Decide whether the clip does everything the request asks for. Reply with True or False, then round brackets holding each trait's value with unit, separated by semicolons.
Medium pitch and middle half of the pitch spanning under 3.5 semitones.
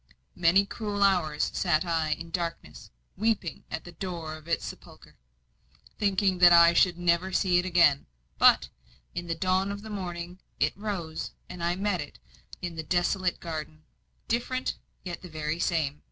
True (175 Hz; 2.5 semitones)